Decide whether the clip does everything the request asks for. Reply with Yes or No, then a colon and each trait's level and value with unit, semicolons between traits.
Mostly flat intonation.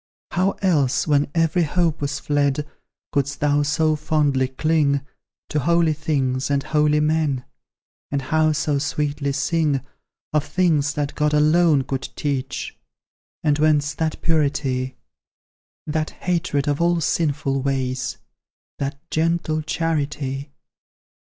Yes: narrow, 2.0 semitones